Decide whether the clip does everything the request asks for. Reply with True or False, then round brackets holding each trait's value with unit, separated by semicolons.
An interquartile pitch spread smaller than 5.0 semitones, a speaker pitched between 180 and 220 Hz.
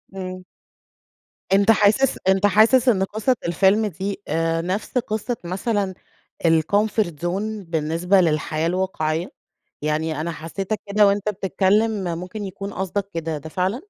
True (3.7 semitones; 190 Hz)